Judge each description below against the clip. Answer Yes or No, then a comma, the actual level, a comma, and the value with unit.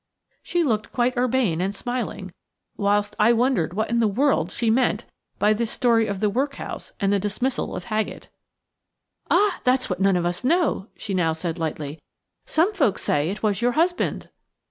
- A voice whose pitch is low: No, high, 215 Hz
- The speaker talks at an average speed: Yes, average, 180 wpm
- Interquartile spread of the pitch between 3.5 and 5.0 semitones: Yes, average, 4.7 semitones